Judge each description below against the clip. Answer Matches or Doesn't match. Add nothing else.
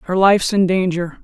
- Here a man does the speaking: Doesn't match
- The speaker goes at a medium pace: Matches